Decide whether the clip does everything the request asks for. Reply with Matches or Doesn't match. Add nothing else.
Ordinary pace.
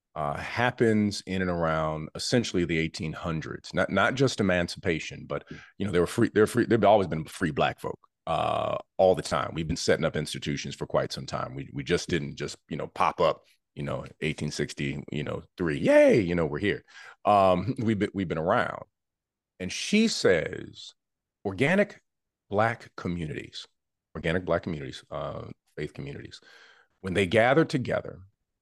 Matches